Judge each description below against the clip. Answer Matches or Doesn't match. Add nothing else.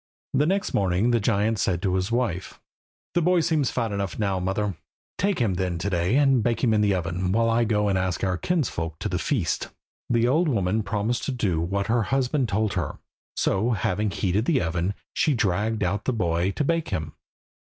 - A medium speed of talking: Doesn't match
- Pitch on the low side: Matches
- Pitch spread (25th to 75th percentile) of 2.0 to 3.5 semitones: Doesn't match